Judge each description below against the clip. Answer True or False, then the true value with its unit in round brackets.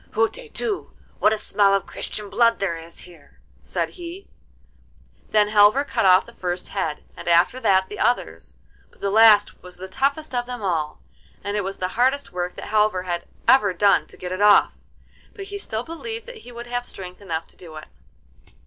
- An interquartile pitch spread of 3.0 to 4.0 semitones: False (5.1 semitones)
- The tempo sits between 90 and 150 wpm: False (195 wpm)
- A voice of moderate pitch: False (205 Hz)